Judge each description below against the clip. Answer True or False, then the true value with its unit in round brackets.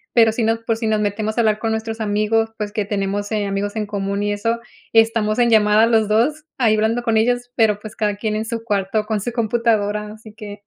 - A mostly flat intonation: True (1.5 semitones)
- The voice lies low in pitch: False (220 Hz)